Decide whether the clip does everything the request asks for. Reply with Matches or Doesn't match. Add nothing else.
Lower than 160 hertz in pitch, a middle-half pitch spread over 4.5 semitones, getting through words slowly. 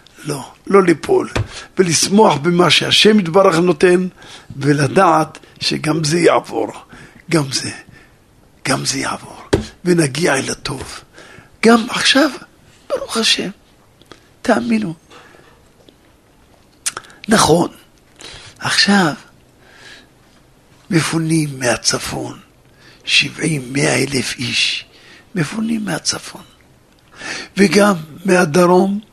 Doesn't match